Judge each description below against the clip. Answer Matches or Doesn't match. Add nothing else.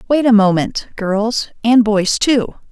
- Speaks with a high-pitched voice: Matches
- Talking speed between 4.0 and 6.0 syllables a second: Doesn't match